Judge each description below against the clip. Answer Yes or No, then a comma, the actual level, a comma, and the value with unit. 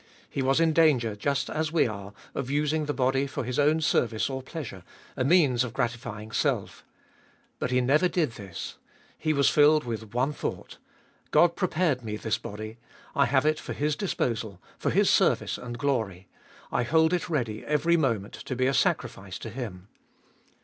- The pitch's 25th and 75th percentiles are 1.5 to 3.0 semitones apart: No, average, 5.1 semitones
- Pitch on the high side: No, low, 130 Hz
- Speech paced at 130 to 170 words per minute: No, average, 185 wpm